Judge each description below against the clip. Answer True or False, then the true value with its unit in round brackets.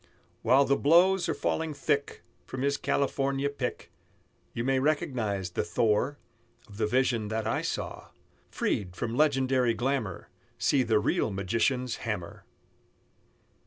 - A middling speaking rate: False (130 wpm)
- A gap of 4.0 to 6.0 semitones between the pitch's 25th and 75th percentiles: True (4.5 semitones)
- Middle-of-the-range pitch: False (125 Hz)